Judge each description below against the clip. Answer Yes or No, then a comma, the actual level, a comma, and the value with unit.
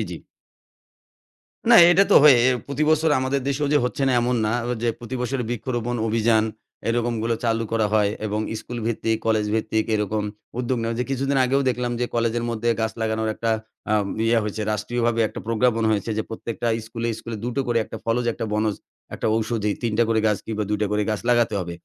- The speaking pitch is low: Yes, low, 115 Hz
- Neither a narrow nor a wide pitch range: No, narrow, 1.9 semitones